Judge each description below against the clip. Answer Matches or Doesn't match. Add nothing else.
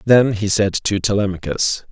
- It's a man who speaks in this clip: Matches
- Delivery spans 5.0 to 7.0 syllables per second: Doesn't match